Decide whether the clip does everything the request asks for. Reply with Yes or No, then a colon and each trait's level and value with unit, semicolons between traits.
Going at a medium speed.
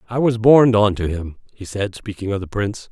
No: fast, 245 wpm